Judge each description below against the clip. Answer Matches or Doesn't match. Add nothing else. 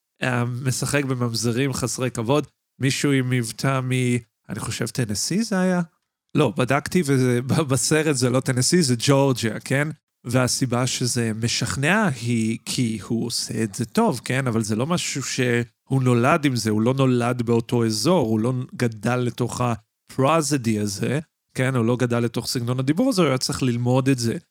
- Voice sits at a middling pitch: Doesn't match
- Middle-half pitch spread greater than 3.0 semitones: Doesn't match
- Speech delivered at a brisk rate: Matches